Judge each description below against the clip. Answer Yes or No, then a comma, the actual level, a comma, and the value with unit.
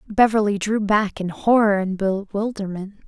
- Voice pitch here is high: Yes, high, 205 Hz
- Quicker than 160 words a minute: No, slow, 135 wpm